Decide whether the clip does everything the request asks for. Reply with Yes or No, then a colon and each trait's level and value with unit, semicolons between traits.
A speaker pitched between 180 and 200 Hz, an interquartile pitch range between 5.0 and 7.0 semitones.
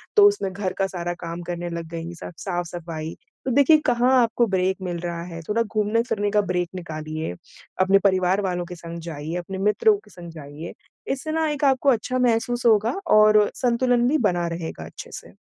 Yes: high, 190 Hz; wide, 5.5 semitones